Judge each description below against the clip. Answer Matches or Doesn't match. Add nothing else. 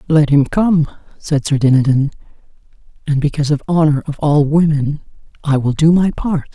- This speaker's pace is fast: Doesn't match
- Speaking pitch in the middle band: Matches